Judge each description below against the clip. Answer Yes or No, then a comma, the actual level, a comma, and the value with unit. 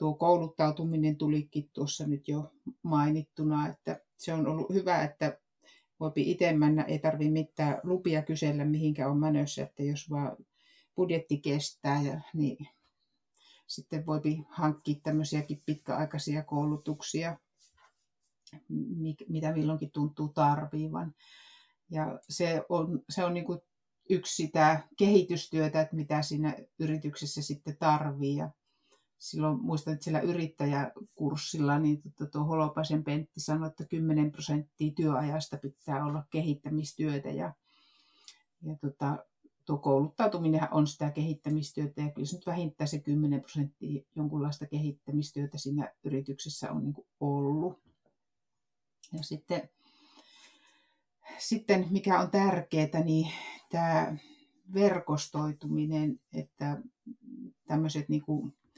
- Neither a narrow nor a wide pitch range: No, narrow, 1.6 semitones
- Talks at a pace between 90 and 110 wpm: Yes, average, 105 wpm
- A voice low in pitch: No, medium, 155 Hz